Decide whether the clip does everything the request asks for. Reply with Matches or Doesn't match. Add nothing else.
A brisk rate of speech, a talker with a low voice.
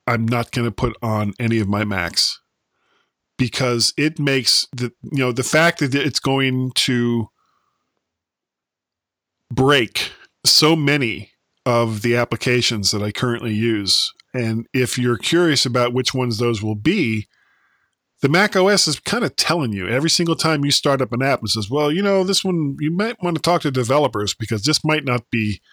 Doesn't match